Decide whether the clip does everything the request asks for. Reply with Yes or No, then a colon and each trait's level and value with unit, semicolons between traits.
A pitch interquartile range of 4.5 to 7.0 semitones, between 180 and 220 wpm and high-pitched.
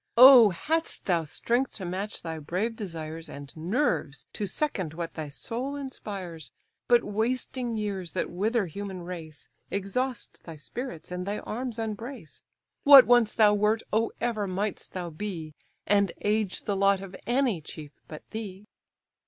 No: average, 5.0 semitones; average, 155 wpm; high, 200 Hz